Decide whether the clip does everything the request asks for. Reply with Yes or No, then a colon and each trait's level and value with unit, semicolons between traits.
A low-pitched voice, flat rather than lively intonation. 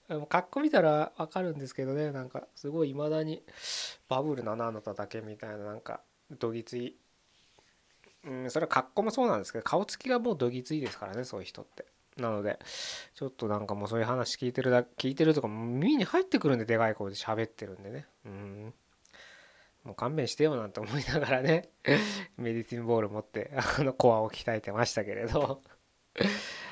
No: low, 130 Hz; wide, 5.6 semitones